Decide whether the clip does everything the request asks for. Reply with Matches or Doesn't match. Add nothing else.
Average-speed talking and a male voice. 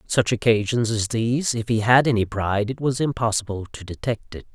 Doesn't match